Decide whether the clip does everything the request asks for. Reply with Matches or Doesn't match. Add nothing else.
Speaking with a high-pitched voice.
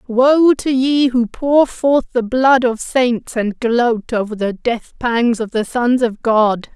Matches